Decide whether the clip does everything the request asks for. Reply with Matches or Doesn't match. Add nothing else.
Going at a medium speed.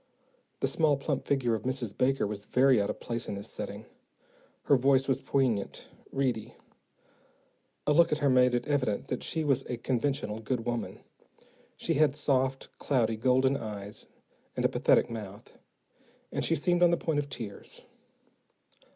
Matches